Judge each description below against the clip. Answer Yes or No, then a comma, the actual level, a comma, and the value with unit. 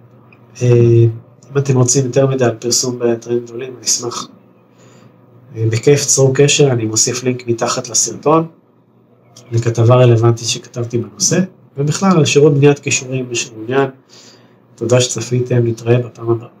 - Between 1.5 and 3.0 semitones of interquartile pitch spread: Yes, narrow, 2.5 semitones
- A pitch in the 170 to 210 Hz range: No, low, 125 Hz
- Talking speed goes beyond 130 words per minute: No, average, 125 wpm